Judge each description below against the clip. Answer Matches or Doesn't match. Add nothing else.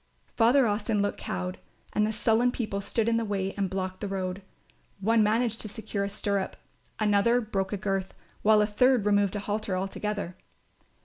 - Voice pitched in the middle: Doesn't match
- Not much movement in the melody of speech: Matches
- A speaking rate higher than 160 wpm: Matches